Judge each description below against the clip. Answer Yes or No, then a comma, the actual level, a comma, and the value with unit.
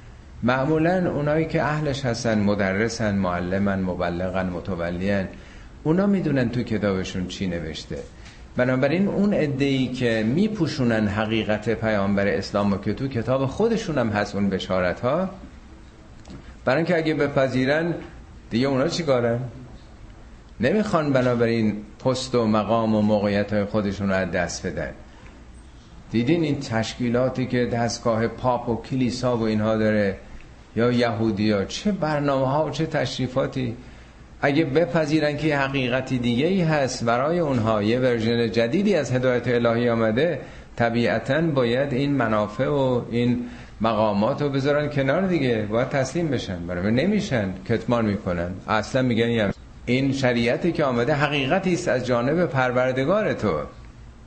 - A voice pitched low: Yes, low, 120 Hz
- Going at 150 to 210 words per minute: No, average, 135 wpm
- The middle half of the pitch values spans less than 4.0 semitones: No, average, 4.6 semitones